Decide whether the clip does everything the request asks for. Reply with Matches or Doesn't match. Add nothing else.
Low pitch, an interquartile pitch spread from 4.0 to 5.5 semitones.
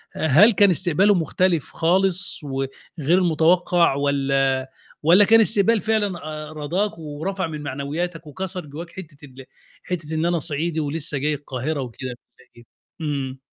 Doesn't match